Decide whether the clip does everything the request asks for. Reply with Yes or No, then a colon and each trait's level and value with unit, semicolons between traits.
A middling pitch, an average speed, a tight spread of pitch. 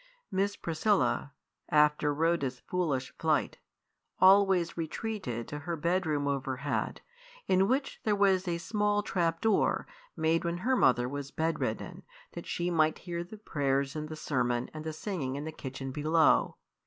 No: medium, 160 Hz; average, 150 wpm; average, 4.7 semitones